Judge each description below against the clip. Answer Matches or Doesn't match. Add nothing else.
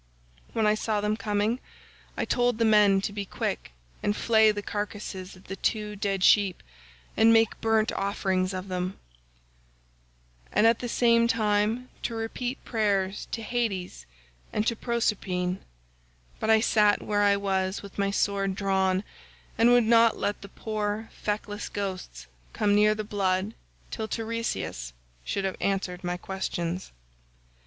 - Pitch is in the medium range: Doesn't match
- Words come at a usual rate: Matches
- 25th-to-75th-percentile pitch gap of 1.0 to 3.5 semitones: Matches